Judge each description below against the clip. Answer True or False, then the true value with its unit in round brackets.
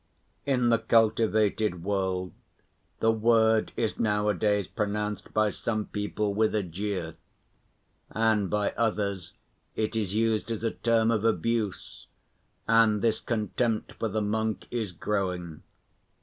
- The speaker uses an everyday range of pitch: False (1.8 semitones)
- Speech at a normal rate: False (125 wpm)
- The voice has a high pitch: False (105 Hz)